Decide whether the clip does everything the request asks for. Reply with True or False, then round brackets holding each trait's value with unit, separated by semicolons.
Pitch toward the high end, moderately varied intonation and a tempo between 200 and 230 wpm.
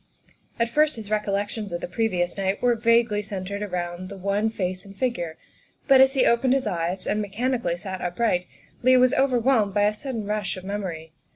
False (205 Hz; 4.1 semitones; 190 wpm)